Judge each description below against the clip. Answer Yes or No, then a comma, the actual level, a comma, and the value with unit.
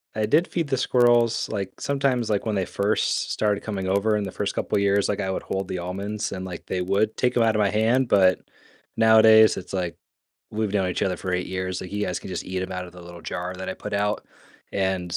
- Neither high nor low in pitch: No, low, 100 Hz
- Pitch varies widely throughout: No, average, 2.8 semitones